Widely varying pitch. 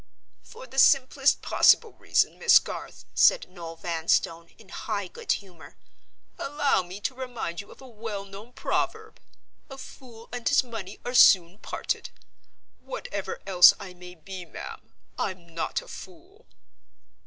Yes: wide, 6.9 semitones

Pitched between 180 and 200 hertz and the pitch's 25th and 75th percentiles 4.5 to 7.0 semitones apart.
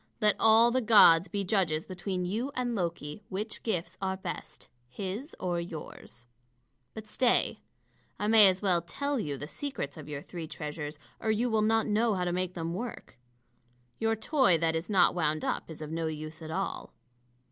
Yes: medium, 185 Hz; average, 5.1 semitones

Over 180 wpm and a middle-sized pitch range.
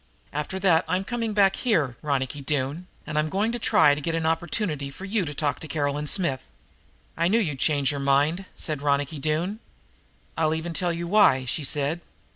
Yes: average, 195 wpm; average, 4.5 semitones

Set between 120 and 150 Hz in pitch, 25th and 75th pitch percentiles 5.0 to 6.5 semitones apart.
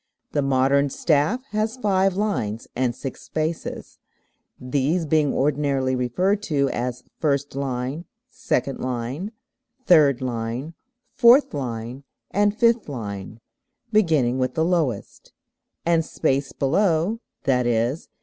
Yes: medium, 140 Hz; average, 5.3 semitones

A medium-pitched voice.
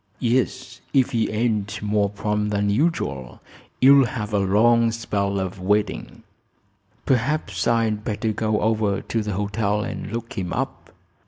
No: low, 105 Hz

